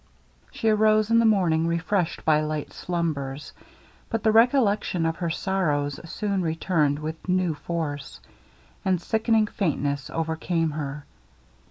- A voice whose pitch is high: No, medium, 170 Hz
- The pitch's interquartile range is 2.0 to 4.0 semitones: No, average, 5.0 semitones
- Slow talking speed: Yes, slow, 130 wpm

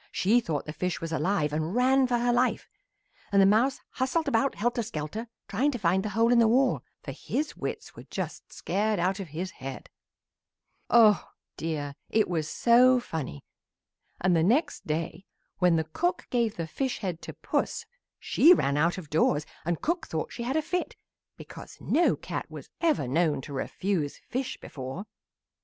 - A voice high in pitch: Yes, high, 200 Hz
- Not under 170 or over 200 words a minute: Yes, average, 180 wpm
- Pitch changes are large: Yes, wide, 7.3 semitones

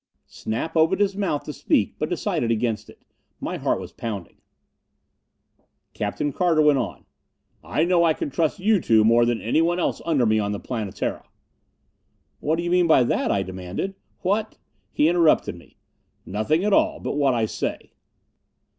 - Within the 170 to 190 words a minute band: Yes, average, 175 wpm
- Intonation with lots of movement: Yes, wide, 7.4 semitones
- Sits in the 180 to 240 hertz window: No, medium, 150 Hz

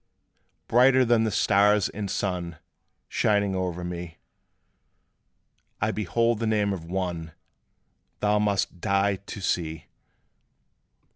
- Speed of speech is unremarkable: No, slow, 110 wpm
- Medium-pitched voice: No, low, 100 Hz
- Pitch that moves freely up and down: No, average, 3.0 semitones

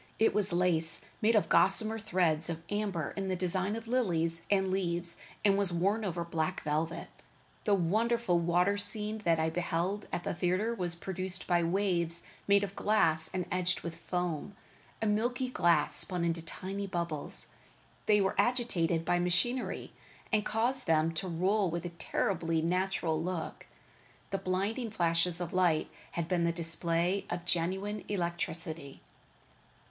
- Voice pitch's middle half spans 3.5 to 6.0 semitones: No, average, 3.1 semitones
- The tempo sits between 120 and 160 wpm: Yes, average, 155 wpm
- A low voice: No, medium, 180 Hz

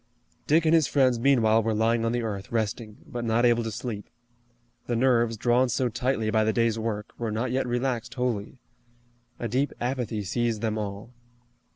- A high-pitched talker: No, low, 115 Hz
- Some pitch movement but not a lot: No, narrow, 2.1 semitones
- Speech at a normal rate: Yes, average, 185 wpm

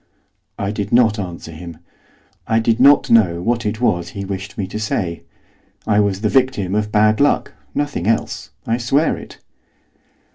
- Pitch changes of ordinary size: Yes, average, 3.3 semitones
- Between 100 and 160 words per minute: No, average, 170 wpm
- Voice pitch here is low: Yes, low, 105 Hz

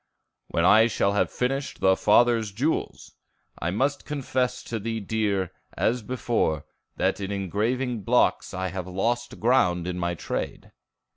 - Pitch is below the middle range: Yes, low, 110 Hz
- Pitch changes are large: No, average, 4.6 semitones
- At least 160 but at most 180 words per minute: No, average, 145 wpm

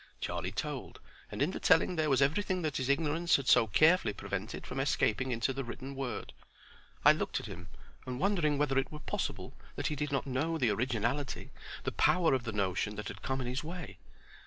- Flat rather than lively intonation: No, average, 4.1 semitones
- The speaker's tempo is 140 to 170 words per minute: No, fast, 205 wpm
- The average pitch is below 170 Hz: Yes, low, 135 Hz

